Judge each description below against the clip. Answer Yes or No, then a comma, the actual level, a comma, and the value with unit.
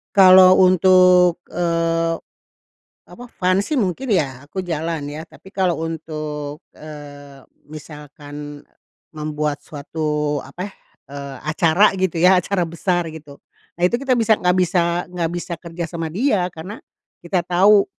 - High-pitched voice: No, medium, 170 Hz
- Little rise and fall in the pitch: No, average, 3.4 semitones